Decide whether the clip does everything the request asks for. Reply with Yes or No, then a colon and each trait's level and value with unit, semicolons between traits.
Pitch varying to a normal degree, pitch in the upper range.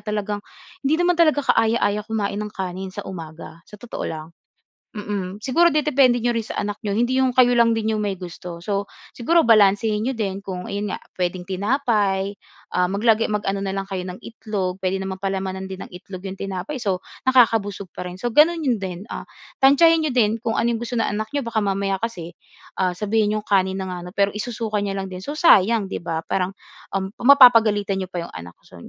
Yes: average, 3.5 semitones; high, 205 Hz